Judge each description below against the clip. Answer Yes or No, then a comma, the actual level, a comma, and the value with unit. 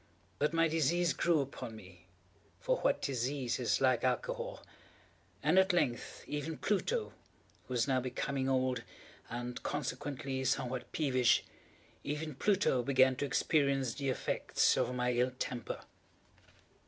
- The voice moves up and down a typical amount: Yes, average, 3.7 semitones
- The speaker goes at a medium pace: No, slow, 120 wpm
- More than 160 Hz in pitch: No, low, 135 Hz